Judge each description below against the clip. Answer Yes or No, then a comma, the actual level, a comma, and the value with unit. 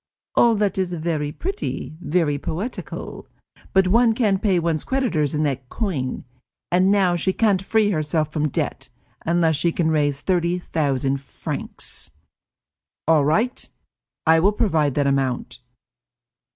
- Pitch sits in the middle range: Yes, medium, 170 Hz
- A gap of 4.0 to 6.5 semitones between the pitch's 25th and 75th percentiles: Yes, average, 4.7 semitones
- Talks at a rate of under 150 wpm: Yes, average, 140 wpm